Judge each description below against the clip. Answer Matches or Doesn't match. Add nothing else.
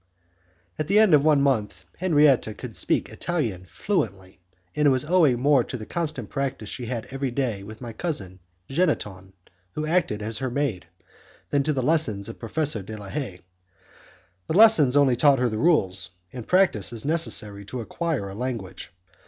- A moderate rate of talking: Matches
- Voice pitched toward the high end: Doesn't match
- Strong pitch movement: Matches